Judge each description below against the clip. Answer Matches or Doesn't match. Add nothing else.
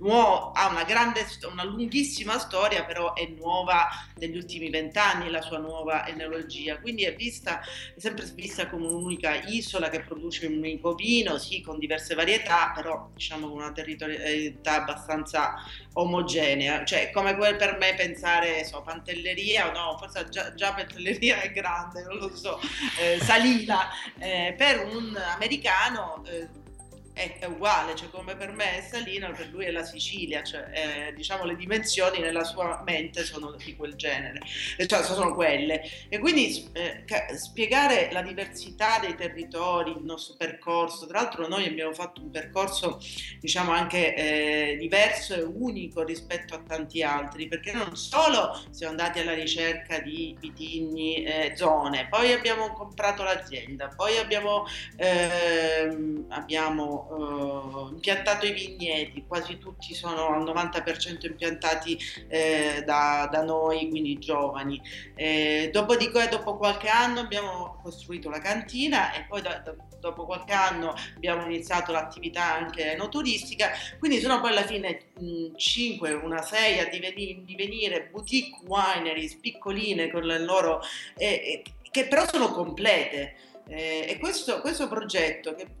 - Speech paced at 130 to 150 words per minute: Matches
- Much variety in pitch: Doesn't match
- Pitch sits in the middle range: Matches